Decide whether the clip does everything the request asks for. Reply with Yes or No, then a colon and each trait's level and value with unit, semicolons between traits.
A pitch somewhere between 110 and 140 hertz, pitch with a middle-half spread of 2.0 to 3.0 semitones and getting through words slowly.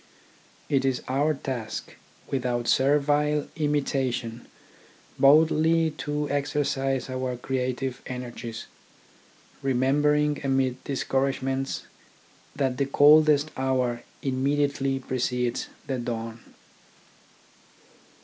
Yes: low, 135 Hz; narrow, 2.4 semitones; slow, 80 wpm